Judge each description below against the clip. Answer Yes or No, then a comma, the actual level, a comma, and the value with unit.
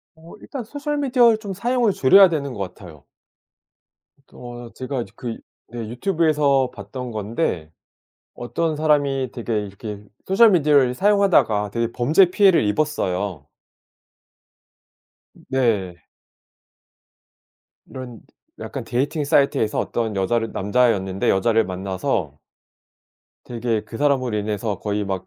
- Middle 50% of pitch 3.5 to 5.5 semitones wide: No, wide, 6.8 semitones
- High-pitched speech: No, low, 120 Hz